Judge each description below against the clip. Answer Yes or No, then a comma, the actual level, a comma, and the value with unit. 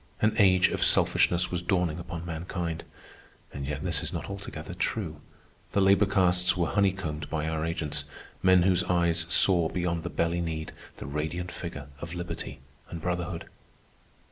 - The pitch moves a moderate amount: No, narrow, 2.3 semitones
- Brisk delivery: No, average, 155 wpm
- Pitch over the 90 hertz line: No, very low, 85 Hz